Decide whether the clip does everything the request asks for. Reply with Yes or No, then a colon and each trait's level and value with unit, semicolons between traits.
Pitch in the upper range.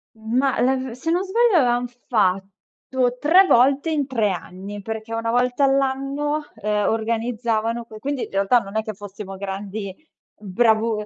Yes: high, 230 Hz